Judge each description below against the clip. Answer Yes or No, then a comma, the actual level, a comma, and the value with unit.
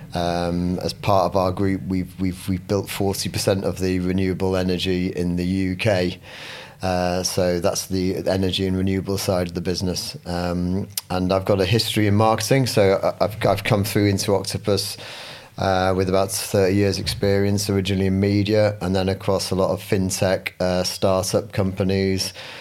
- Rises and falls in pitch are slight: Yes, narrow, 1.6 semitones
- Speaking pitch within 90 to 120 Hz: Yes, very low, 95 Hz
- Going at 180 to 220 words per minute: No, average, 165 wpm